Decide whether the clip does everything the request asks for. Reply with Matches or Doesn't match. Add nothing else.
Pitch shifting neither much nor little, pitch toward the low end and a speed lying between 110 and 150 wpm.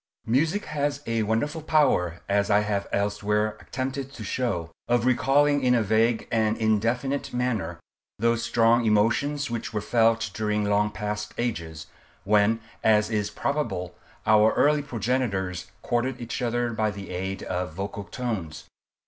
Matches